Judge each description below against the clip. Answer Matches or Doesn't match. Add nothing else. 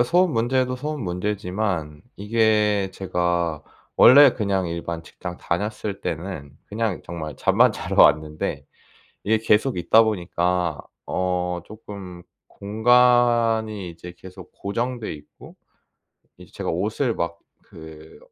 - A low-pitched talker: Matches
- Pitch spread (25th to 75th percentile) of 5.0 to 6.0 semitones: Doesn't match